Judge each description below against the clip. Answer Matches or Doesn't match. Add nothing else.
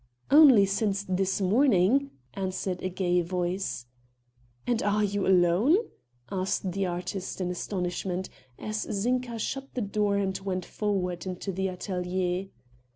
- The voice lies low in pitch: Doesn't match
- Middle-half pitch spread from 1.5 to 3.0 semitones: Matches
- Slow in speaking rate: Matches